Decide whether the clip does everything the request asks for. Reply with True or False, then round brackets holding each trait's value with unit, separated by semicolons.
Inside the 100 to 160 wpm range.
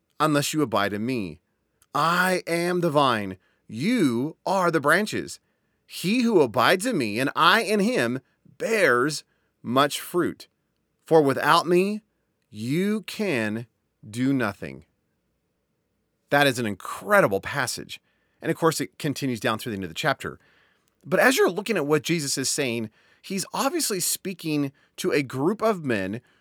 True (150 wpm)